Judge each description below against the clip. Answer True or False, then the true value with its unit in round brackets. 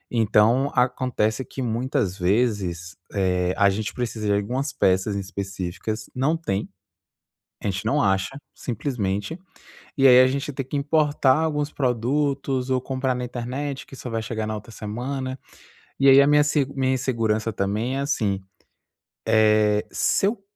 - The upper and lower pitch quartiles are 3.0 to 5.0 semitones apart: True (4.5 semitones)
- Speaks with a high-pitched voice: False (120 Hz)